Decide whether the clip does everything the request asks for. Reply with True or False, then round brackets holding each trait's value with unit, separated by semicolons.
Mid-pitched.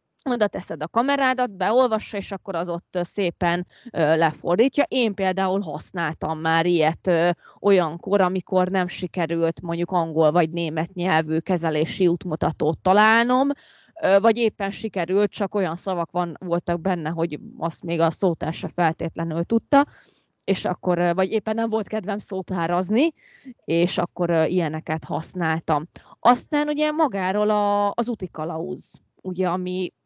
True (180 Hz)